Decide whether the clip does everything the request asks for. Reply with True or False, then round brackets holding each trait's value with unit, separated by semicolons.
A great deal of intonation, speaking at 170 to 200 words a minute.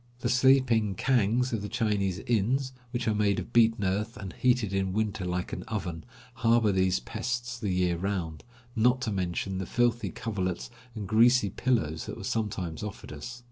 False (4.2 semitones; 180 wpm)